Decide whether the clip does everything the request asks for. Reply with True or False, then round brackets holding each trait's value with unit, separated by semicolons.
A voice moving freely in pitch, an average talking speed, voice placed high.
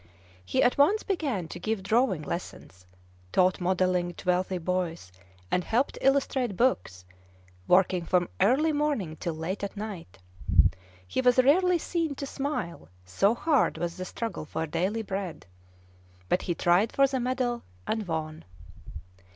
True (6.8 semitones; 145 wpm; 195 Hz)